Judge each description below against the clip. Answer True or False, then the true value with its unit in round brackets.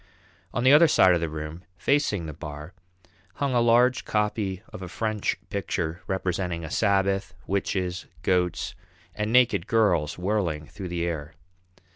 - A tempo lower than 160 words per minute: True (150 wpm)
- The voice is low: True (95 Hz)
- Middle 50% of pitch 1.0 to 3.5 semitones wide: False (4.2 semitones)